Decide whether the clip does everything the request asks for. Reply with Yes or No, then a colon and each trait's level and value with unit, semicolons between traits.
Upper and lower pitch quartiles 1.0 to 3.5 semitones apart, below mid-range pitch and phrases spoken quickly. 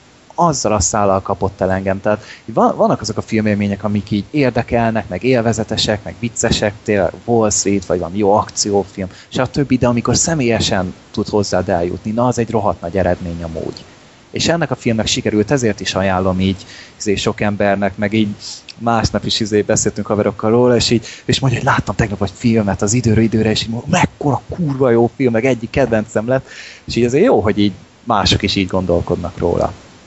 Yes: average, 2.9 semitones; low, 105 Hz; fast, 190 wpm